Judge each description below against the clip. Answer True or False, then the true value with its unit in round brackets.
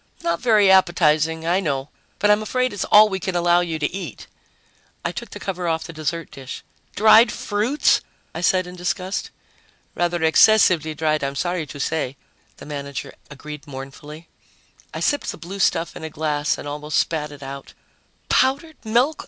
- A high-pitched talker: False (170 Hz)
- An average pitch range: True (4.5 semitones)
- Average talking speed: True (175 wpm)